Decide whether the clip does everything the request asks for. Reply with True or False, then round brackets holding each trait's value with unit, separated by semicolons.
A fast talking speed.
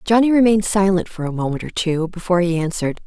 True (215 wpm)